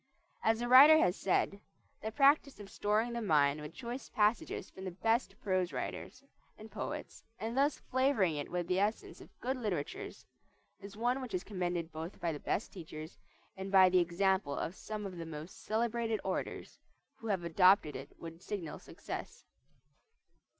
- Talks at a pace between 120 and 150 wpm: No, average, 170 wpm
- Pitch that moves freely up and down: No, average, 4.9 semitones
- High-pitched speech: Yes, high, 195 Hz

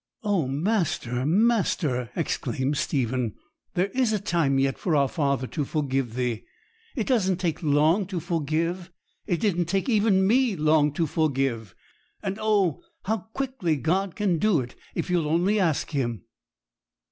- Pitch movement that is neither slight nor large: No, wide, 6.0 semitones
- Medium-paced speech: Yes, average, 150 wpm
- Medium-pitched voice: Yes, medium, 165 Hz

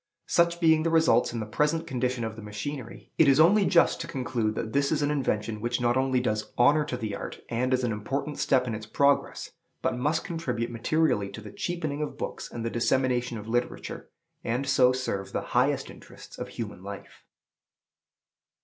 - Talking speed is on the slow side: No, average, 195 wpm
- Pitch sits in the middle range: No, low, 125 Hz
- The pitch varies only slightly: No, average, 4.7 semitones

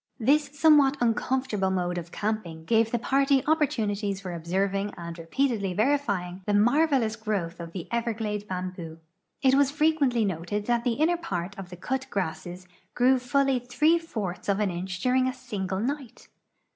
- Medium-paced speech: Yes, average, 170 wpm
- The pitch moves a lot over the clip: Yes, wide, 6.2 semitones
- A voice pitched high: Yes, high, 215 Hz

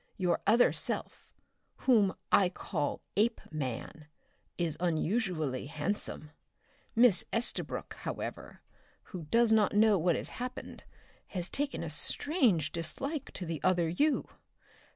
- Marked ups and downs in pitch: Yes, wide, 6.1 semitones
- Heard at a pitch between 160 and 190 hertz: Yes, medium, 185 Hz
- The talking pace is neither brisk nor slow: No, slow, 115 wpm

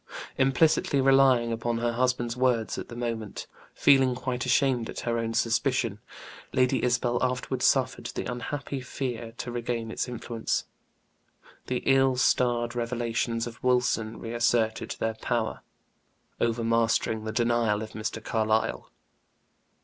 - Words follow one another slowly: Yes, slow, 125 wpm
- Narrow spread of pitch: Yes, narrow, 1.8 semitones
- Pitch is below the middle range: Yes, low, 120 Hz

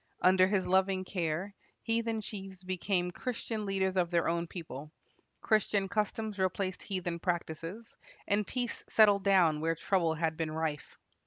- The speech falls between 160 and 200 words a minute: No, average, 145 wpm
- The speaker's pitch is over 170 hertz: Yes, medium, 185 Hz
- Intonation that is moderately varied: Yes, average, 3.2 semitones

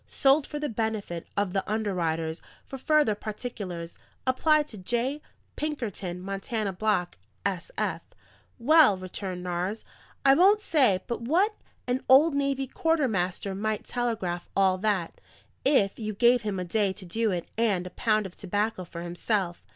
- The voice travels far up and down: Yes, wide, 5.9 semitones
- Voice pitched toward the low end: No, high, 215 Hz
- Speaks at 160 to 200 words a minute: No, average, 150 wpm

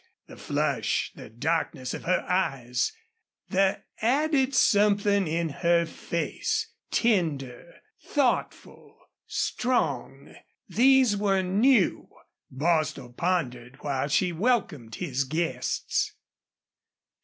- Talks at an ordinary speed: No, slow, 90 wpm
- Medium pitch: Yes, medium, 175 Hz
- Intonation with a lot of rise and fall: Yes, wide, 7.1 semitones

